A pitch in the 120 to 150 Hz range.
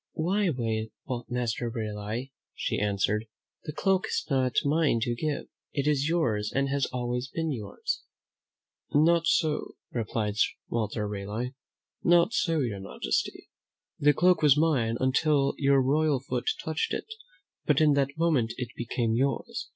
Yes: low, 135 Hz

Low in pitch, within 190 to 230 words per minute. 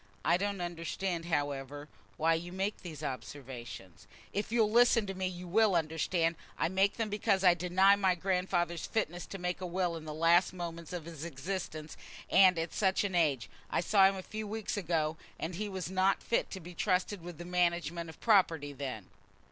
No: medium, 175 Hz; average, 195 wpm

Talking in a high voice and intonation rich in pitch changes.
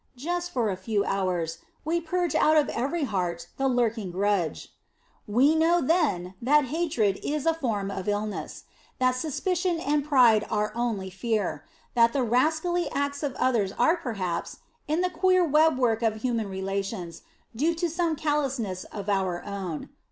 Yes: high, 245 Hz; wide, 7.8 semitones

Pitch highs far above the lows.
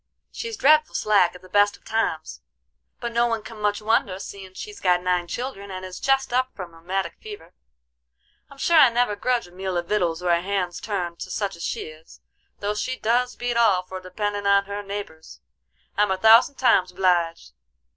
No: average, 4.3 semitones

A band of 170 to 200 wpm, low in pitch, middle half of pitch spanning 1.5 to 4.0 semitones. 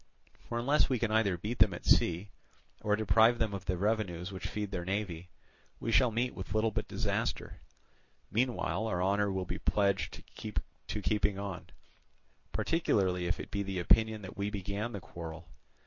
Yes: average, 175 wpm; low, 100 Hz; average, 3.0 semitones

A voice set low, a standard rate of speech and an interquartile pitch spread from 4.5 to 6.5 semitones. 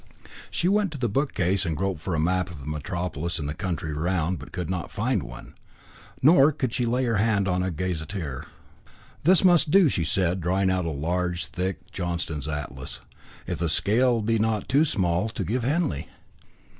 Yes: very low, 90 Hz; average, 190 wpm; wide, 5.5 semitones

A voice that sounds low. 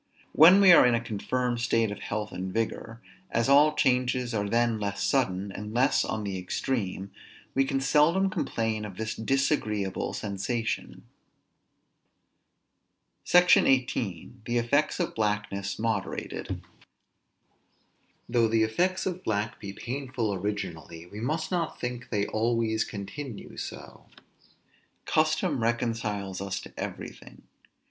Yes: low, 115 Hz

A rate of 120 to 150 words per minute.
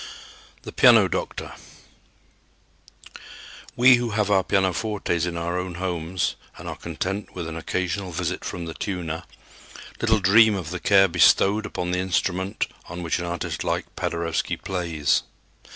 Yes: average, 145 wpm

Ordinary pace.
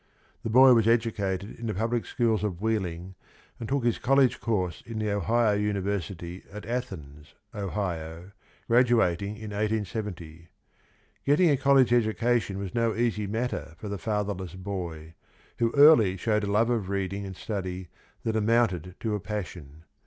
Yes: average, 155 wpm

